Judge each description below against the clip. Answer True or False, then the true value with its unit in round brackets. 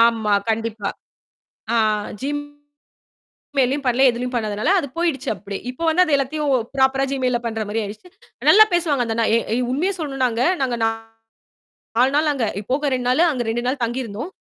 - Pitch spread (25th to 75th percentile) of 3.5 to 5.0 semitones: True (4.0 semitones)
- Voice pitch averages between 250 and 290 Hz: True (255 Hz)